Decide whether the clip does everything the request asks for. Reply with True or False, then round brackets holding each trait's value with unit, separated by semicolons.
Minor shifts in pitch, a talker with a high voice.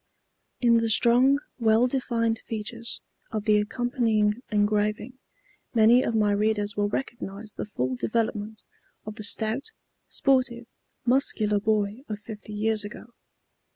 True (2.1 semitones; 220 Hz)